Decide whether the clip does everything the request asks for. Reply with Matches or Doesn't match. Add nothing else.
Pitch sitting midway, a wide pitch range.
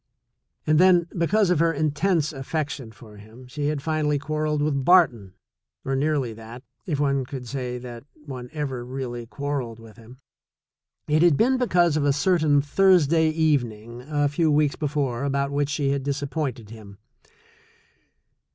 Doesn't match